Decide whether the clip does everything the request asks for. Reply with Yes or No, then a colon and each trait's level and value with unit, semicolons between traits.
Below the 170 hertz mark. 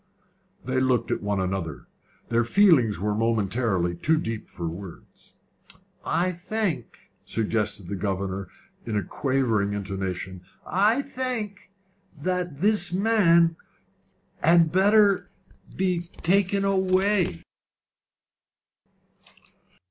Yes: low, 135 Hz